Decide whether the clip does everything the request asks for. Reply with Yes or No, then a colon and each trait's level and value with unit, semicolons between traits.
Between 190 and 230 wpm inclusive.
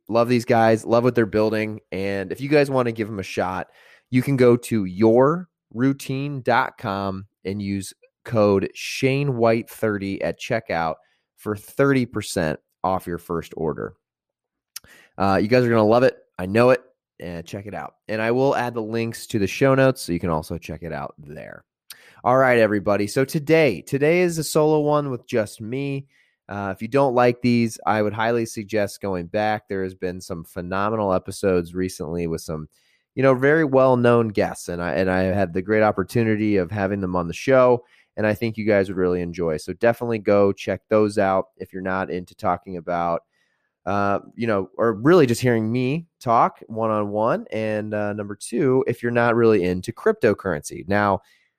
Yes: average, 195 wpm